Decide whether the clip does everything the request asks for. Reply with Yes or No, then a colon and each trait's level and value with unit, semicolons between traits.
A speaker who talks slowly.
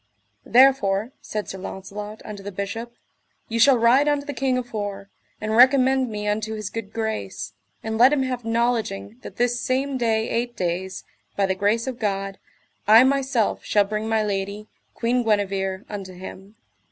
No: average, 165 wpm